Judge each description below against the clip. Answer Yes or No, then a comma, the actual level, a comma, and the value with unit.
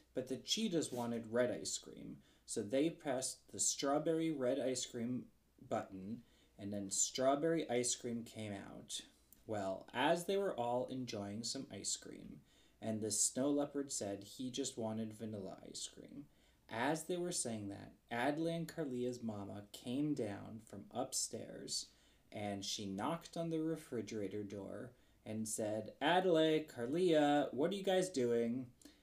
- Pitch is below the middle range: Yes, low, 125 Hz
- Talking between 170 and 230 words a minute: No, average, 150 wpm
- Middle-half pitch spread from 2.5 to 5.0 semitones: No, wide, 5.5 semitones